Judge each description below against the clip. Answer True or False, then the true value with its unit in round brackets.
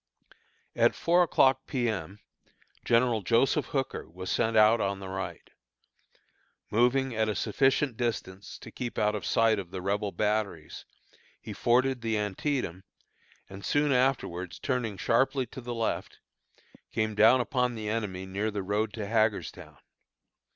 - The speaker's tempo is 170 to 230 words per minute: False (145 wpm)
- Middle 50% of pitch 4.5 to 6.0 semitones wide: False (3.8 semitones)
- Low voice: True (110 Hz)